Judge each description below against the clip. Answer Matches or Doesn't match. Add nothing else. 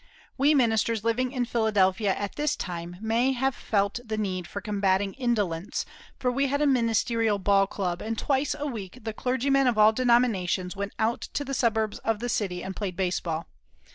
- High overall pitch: Matches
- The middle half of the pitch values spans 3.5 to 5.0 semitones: Matches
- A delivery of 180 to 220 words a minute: Matches